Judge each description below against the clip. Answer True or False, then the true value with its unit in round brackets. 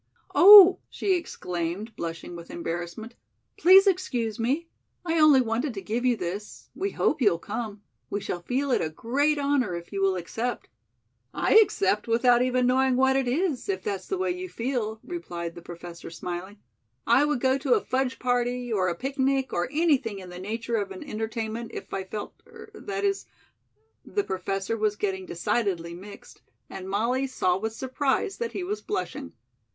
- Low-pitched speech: False (235 Hz)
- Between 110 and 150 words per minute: False (180 wpm)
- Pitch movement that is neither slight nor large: False (6.7 semitones)